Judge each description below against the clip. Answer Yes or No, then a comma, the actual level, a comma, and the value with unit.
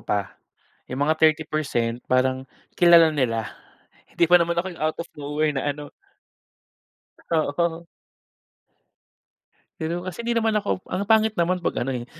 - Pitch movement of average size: Yes, average, 4.5 semitones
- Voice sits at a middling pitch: Yes, medium, 160 Hz